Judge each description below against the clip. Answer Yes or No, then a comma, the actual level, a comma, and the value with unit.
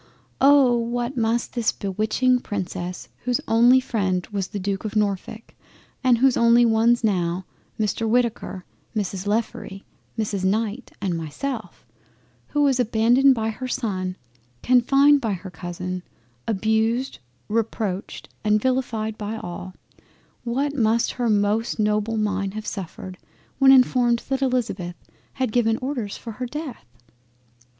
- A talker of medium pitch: No, high, 225 Hz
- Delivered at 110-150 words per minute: Yes, slow, 135 wpm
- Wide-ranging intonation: No, average, 3.5 semitones